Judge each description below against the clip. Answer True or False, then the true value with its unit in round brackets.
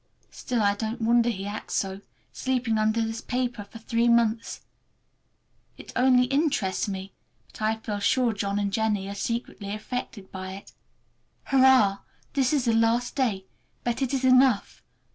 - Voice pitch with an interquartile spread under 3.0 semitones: False (3.5 semitones)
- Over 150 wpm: True (160 wpm)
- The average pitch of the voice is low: False (225 Hz)